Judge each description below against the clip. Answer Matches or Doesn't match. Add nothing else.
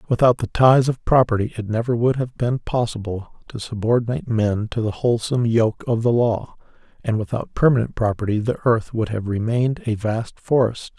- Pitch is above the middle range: Doesn't match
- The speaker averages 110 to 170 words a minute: Doesn't match